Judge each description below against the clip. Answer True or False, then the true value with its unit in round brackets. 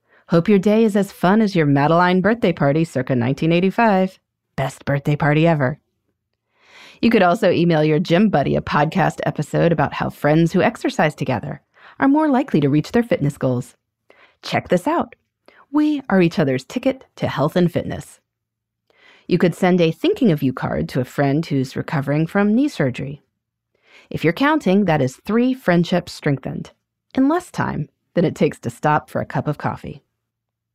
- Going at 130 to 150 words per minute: False (175 wpm)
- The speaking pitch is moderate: True (165 Hz)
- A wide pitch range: True (6.2 semitones)